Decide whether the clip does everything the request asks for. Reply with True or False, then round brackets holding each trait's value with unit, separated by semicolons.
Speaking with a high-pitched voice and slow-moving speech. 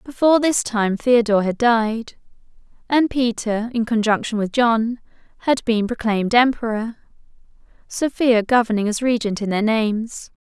True (230 Hz; 130 wpm)